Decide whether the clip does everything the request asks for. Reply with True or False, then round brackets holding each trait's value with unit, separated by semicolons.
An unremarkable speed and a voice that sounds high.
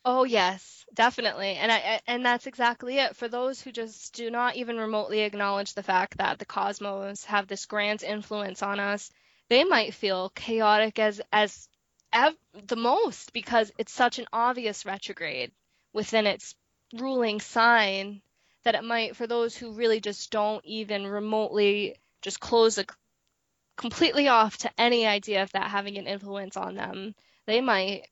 True (160 wpm; 215 Hz)